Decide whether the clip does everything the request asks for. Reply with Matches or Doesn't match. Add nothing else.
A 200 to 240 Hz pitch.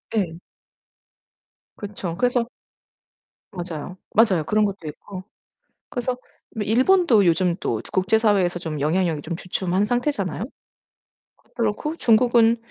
Matches